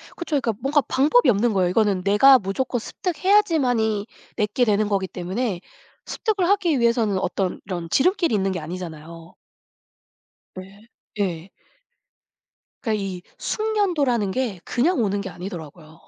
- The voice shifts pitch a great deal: Yes, wide, 6.3 semitones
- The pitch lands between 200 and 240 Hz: Yes, high, 215 Hz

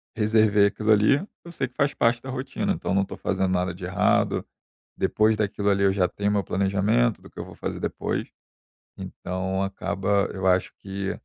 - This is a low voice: Yes, low, 100 Hz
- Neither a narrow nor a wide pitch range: No, narrow, 2.2 semitones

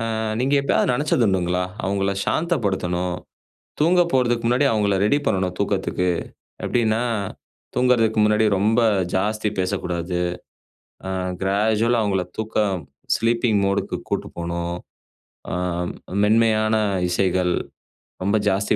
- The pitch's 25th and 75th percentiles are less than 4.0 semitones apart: Yes, average, 3.5 semitones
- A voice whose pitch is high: No, low, 105 Hz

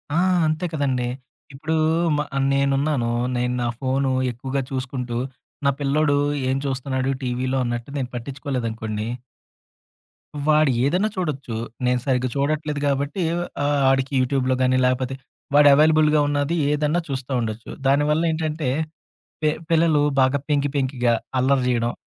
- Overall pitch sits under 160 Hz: Yes, low, 135 Hz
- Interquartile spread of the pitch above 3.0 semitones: No, average, 2.7 semitones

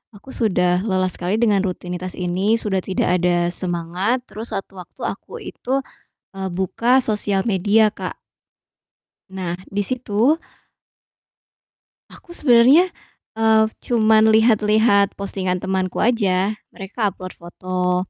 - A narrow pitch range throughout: No, average, 3.3 semitones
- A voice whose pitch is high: Yes, high, 200 Hz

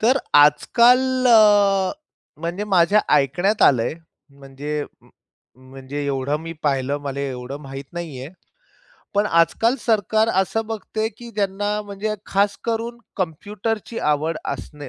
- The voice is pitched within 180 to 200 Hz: Yes, medium, 185 Hz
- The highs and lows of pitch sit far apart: Yes, wide, 7.0 semitones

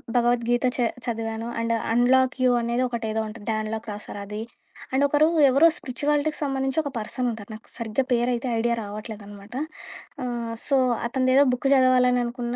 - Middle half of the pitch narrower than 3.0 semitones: Yes, narrow, 2.5 semitones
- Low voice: No, high, 240 Hz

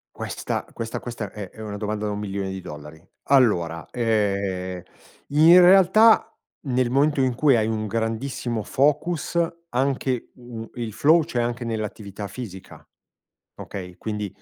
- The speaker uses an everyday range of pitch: Yes, average, 4.5 semitones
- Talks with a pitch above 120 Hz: No, low, 115 Hz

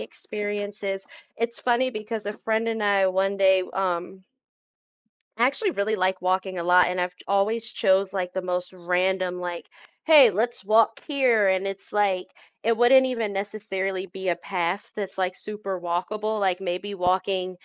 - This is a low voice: No, high, 195 Hz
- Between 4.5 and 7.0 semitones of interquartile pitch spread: No, narrow, 2.6 semitones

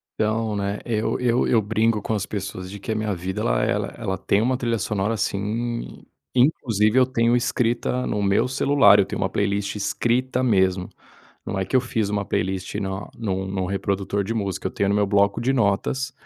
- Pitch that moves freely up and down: No, average, 3.2 semitones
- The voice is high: No, low, 105 Hz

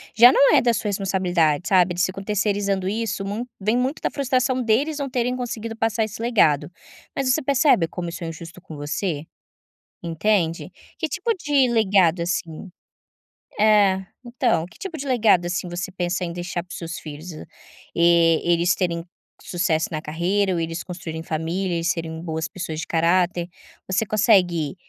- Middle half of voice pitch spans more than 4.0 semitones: Yes, average, 4.9 semitones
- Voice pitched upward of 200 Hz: No, medium, 185 Hz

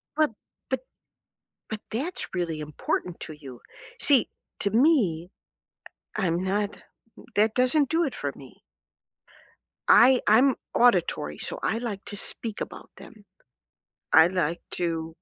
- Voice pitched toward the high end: Yes, high, 205 Hz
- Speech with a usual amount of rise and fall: No, wide, 6.6 semitones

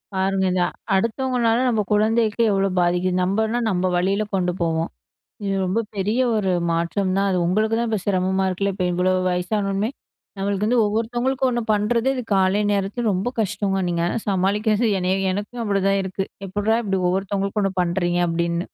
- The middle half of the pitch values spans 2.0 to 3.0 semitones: Yes, average, 2.7 semitones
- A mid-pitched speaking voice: No, high, 195 Hz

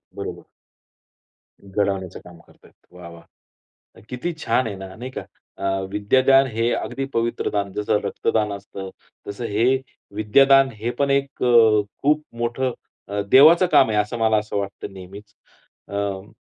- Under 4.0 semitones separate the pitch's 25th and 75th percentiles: No, average, 4.4 semitones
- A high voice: No, low, 105 Hz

